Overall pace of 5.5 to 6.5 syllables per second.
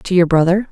Yes: 6.0 syllables/s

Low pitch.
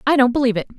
No: very high, 250 Hz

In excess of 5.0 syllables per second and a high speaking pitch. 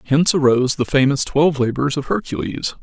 No: 6.1 syllables/s; medium, 140 Hz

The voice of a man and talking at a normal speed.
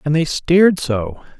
Yes: male; average, 170 wpm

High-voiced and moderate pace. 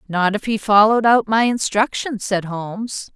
Yes: high, 215 Hz; average, 170 wpm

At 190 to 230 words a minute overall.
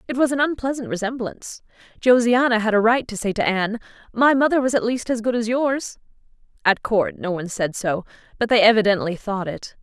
Yes: average, 200 wpm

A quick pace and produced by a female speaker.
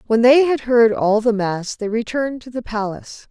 Yes: fast, 220 wpm; female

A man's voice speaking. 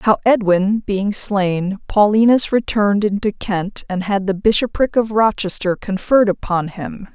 No: female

